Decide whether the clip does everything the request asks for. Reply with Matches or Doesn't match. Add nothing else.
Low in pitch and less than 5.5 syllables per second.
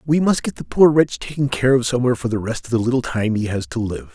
Doesn't match